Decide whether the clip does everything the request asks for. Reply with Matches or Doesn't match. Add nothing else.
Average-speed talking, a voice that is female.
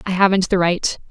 Doesn't match